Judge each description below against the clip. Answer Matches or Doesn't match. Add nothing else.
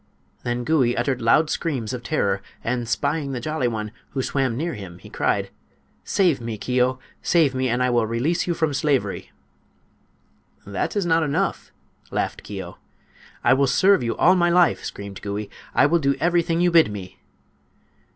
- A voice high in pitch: Doesn't match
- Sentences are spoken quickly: Doesn't match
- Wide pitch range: Matches